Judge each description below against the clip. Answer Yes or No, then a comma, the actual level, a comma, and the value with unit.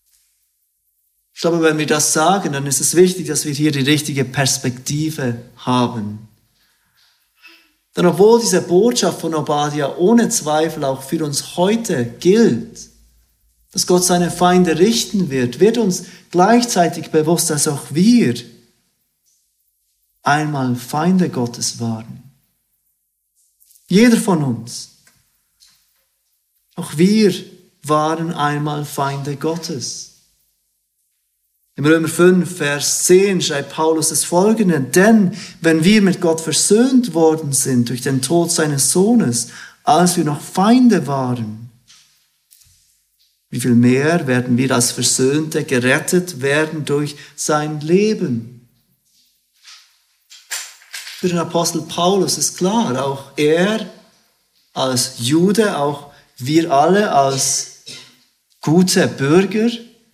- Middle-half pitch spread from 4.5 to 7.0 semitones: Yes, average, 5.0 semitones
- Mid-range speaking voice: Yes, medium, 155 Hz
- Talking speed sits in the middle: No, slow, 110 wpm